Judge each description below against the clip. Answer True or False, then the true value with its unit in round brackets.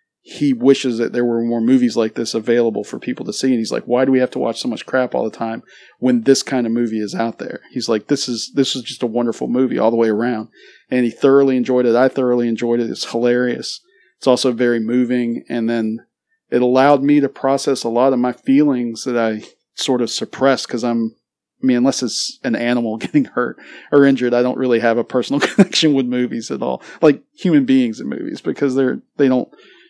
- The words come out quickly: True (230 wpm)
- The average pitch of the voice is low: True (125 Hz)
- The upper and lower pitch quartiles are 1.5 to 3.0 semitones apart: True (2.4 semitones)